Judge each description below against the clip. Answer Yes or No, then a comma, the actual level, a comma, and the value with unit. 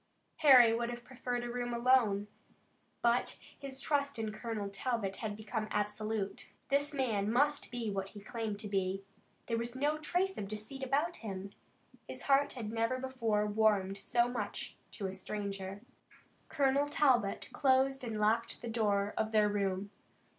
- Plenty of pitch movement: No, average, 4.0 semitones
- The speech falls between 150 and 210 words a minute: Yes, average, 160 wpm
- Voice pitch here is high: Yes, high, 230 Hz